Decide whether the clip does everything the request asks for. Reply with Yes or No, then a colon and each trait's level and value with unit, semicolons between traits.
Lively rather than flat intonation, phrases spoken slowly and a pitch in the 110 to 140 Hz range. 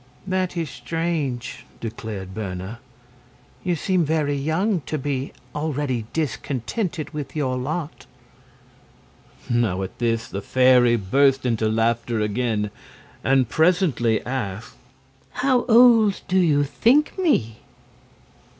Yes: wide, 6.2 semitones; slow, 110 wpm; low, 135 Hz